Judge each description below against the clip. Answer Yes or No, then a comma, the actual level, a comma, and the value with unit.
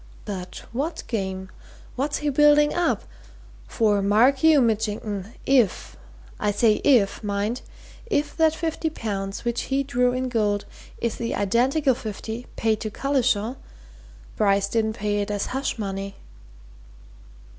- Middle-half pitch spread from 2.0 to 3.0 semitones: No, average, 4.6 semitones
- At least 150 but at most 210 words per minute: No, slow, 135 wpm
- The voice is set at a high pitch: Yes, high, 230 Hz